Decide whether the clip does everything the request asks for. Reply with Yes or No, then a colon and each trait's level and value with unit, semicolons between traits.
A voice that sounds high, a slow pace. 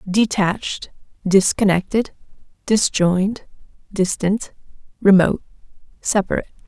Yes: high, 200 Hz; slow, 55 wpm